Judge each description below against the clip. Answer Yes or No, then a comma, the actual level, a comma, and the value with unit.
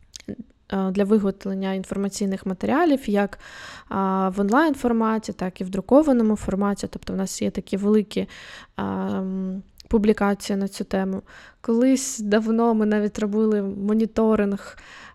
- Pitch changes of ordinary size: No, narrow, 2.3 semitones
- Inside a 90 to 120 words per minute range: Yes, average, 110 wpm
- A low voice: No, high, 205 Hz